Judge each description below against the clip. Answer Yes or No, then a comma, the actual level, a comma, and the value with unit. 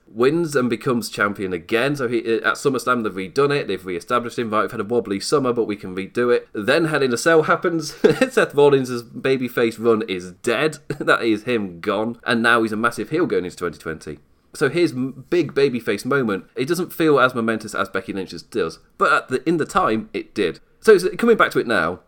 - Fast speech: Yes, fast, 215 wpm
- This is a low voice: Yes, low, 120 Hz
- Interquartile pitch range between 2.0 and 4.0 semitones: No, average, 4.9 semitones